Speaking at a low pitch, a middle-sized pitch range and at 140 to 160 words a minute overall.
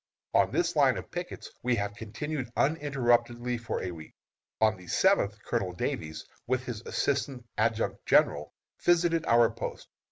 Yes: low, 120 Hz; average, 4.8 semitones; average, 150 wpm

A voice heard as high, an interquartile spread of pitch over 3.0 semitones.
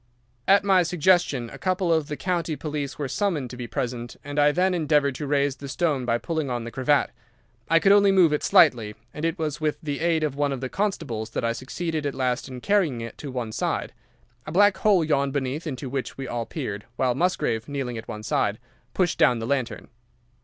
No: medium, 145 Hz; average, 4.8 semitones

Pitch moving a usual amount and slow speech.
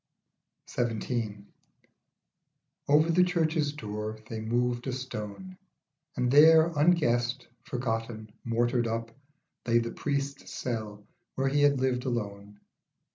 Yes: average, 4.2 semitones; slow, 110 wpm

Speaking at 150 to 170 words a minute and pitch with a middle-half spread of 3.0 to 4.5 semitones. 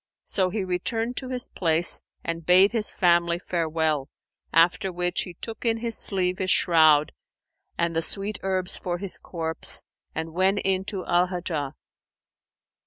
No: average, 155 wpm; narrow, 2.6 semitones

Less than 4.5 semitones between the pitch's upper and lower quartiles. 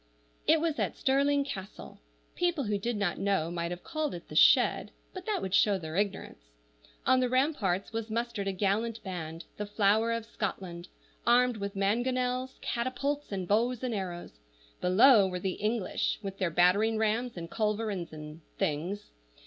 No: average, 4.9 semitones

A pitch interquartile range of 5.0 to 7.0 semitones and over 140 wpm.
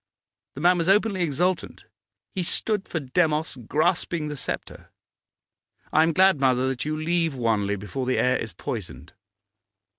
Yes: wide, 5.4 semitones; average, 150 wpm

